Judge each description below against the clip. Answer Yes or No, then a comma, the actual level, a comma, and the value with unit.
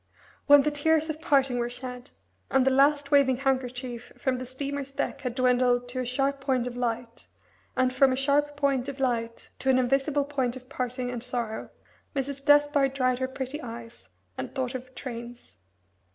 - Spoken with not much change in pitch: Yes, narrow, 2.1 semitones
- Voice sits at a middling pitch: No, very high, 260 Hz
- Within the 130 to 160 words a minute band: No, average, 180 wpm